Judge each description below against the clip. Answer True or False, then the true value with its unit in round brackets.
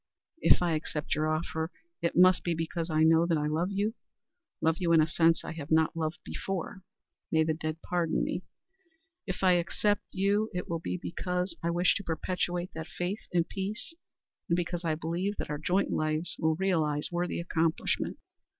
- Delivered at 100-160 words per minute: False (185 wpm)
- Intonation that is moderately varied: False (2.1 semitones)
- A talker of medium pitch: True (170 Hz)